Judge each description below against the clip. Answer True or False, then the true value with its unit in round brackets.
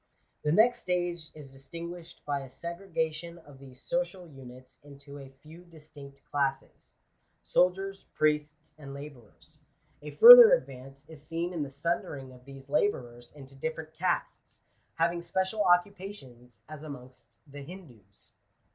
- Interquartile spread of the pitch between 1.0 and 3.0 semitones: False (4.1 semitones)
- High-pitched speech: False (150 Hz)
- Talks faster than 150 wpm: False (140 wpm)